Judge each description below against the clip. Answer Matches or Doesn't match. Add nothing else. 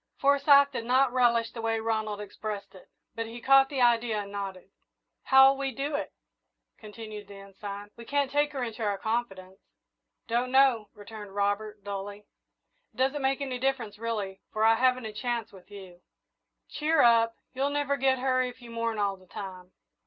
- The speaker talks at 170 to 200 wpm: Matches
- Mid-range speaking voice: Doesn't match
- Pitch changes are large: Doesn't match